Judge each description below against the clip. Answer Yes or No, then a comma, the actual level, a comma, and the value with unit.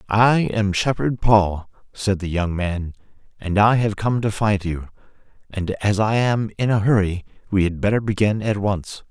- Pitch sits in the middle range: No, low, 105 Hz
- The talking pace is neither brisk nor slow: Yes, average, 185 wpm